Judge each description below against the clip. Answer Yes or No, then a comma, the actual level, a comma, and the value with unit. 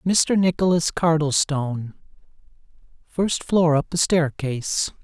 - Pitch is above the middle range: No, medium, 160 Hz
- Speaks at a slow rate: Yes, slow, 95 wpm